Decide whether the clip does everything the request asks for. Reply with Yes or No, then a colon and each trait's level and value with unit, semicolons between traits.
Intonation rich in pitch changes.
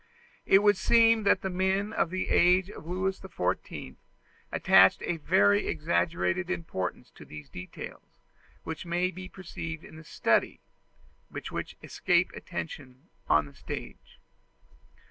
Yes: wide, 7.0 semitones